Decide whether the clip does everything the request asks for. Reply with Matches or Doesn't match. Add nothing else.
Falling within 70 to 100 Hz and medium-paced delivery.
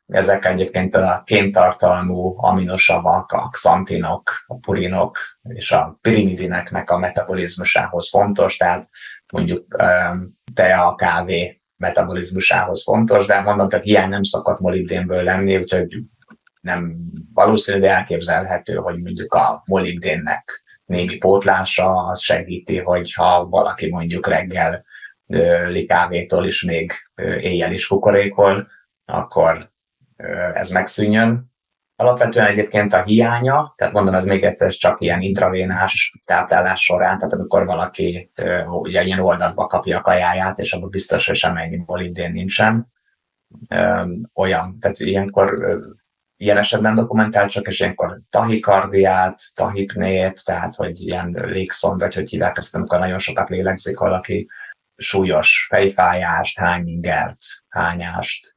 Matches